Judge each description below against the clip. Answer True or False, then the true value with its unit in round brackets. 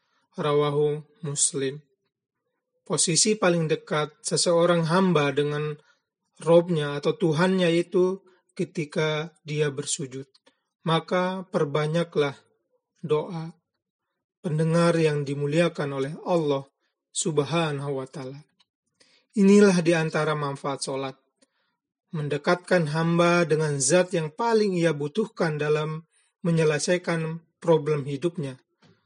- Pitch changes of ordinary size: True (3.4 semitones)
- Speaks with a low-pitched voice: False (165 Hz)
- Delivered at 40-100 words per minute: True (90 wpm)